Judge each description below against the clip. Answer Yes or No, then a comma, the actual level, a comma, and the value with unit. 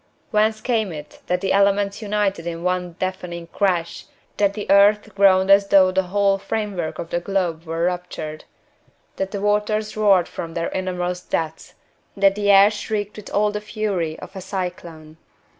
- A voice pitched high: Yes, high, 195 Hz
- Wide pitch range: No, average, 2.7 semitones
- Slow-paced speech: No, average, 170 wpm